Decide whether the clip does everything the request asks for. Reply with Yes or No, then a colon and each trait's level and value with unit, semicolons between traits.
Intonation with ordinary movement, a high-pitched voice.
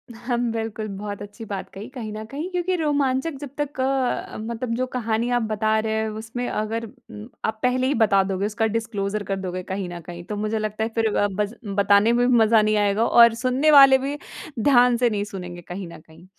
Yes: average, 3.4 semitones; high, 220 Hz